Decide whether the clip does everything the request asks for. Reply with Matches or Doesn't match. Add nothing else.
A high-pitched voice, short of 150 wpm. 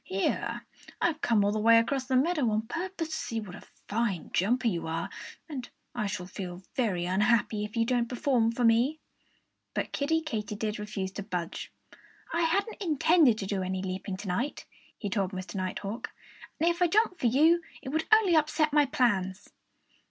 Doesn't match